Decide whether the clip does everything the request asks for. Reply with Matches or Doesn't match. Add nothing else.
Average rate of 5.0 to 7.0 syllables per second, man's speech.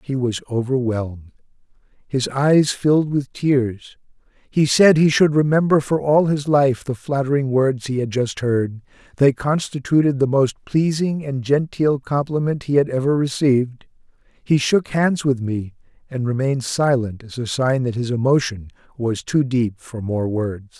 Doesn't match